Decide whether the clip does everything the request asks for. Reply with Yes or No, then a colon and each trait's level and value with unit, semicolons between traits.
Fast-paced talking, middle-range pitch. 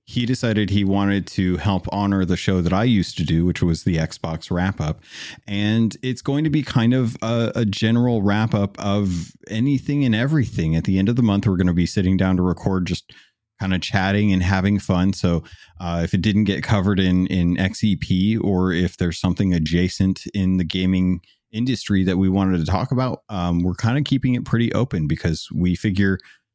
No: fast, 210 wpm; very low, 95 Hz